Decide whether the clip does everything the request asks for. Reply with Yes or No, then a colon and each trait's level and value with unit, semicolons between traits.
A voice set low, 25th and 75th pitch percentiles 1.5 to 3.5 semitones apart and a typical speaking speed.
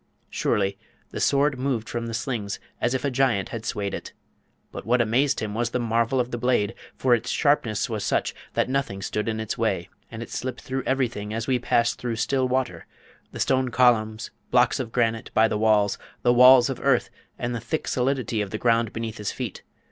No: low, 120 Hz; narrow, 2.6 semitones; fast, 210 wpm